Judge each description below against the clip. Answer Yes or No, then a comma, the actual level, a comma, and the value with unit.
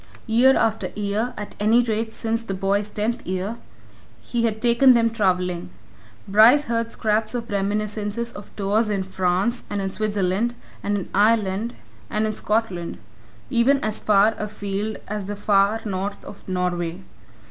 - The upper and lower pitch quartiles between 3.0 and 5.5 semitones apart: No, narrow, 2.6 semitones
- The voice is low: No, high, 210 Hz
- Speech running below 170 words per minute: Yes, average, 150 wpm